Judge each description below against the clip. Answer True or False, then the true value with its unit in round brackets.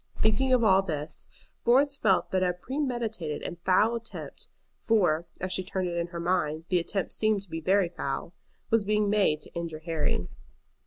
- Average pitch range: True (4.2 semitones)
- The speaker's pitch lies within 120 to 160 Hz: False (185 Hz)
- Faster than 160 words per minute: True (180 wpm)